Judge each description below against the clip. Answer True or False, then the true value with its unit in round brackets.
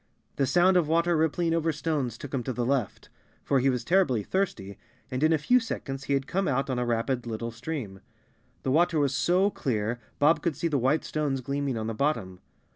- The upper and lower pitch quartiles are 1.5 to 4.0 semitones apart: False (4.8 semitones)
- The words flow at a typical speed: False (215 wpm)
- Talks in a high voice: False (140 Hz)